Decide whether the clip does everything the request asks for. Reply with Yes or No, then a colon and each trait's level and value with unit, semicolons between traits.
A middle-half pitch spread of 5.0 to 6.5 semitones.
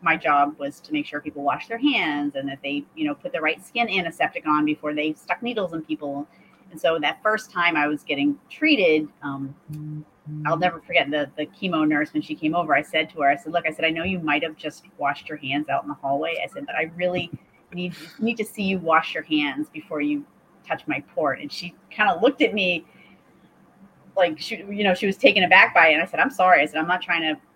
Yes: wide, 5.5 semitones